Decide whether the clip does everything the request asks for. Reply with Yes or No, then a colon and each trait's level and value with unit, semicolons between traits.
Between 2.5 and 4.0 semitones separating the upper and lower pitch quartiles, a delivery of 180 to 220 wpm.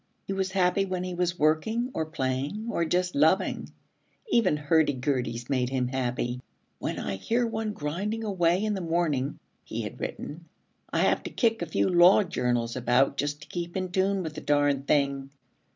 No: wide, 5.5 semitones; average, 185 wpm